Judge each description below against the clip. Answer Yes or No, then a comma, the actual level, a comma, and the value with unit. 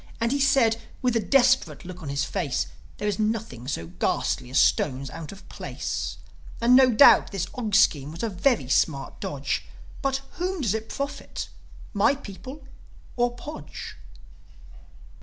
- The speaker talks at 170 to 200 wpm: No, average, 160 wpm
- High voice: Yes, high, 215 Hz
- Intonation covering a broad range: Yes, wide, 8.5 semitones